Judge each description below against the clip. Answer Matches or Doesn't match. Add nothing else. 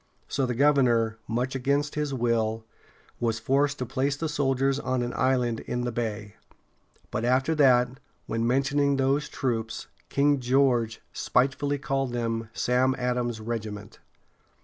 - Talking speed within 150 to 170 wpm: Doesn't match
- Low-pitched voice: Matches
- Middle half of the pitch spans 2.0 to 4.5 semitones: Matches